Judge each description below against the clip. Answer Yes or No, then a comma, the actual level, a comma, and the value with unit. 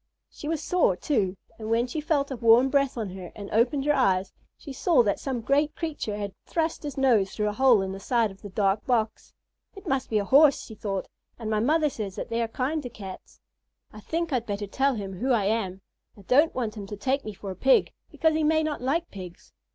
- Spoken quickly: Yes, fast, 240 wpm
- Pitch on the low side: No, high, 235 Hz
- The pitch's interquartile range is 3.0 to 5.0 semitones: No, wide, 5.4 semitones